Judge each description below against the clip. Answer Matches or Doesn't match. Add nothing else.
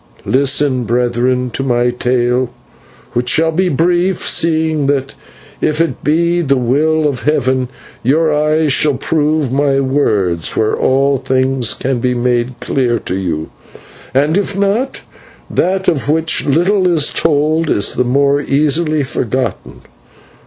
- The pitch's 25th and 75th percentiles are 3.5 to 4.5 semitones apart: Matches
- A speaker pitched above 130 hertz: Matches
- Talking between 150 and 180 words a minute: Doesn't match